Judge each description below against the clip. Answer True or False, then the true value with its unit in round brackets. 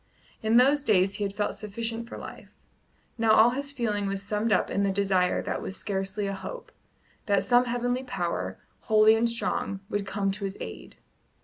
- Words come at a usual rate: True (190 wpm)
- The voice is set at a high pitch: True (210 Hz)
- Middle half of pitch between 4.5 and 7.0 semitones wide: False (3.0 semitones)